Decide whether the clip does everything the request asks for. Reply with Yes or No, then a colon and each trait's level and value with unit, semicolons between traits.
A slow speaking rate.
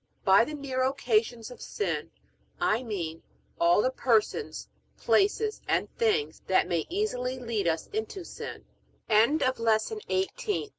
Yes: slow, 115 wpm